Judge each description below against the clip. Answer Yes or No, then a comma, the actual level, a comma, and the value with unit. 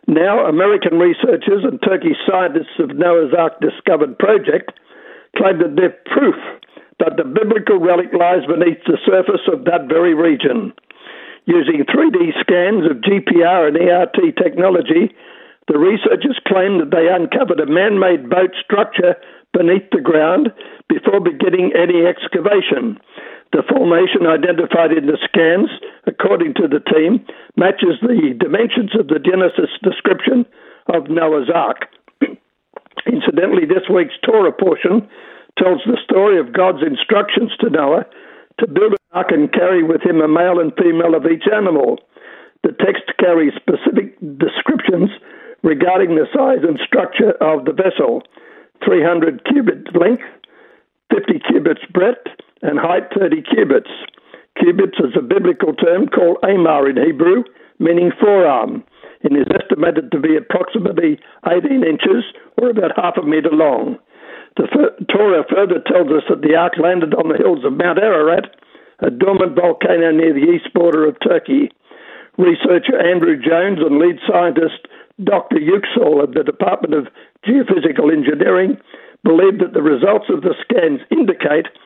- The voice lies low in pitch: No, high, 195 Hz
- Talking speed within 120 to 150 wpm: Yes, average, 145 wpm